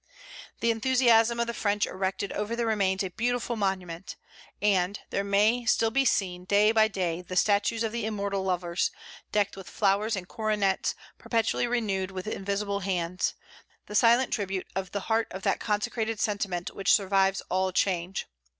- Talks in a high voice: Yes, high, 200 Hz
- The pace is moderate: Yes, average, 165 wpm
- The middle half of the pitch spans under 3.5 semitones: Yes, average, 2.8 semitones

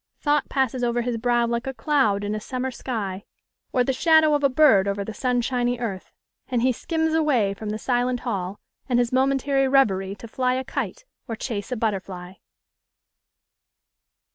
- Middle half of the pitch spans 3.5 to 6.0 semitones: Yes, average, 3.9 semitones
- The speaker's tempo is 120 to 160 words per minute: No, average, 175 wpm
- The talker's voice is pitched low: No, high, 245 Hz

